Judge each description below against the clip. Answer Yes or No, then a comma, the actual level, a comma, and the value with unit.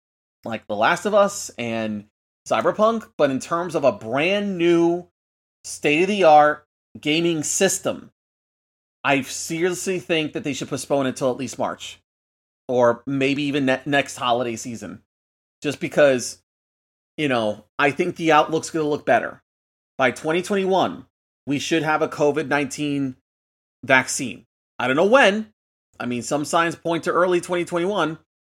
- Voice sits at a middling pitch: Yes, medium, 145 Hz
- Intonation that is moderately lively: No, wide, 6.2 semitones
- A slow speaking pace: No, average, 150 wpm